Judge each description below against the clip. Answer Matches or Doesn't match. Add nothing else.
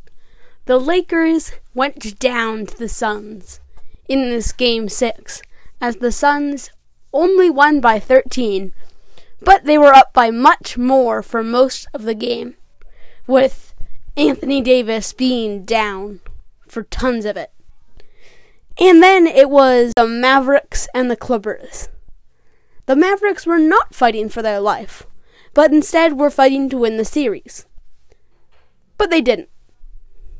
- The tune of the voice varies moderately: Matches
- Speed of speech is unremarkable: Doesn't match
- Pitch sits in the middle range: Doesn't match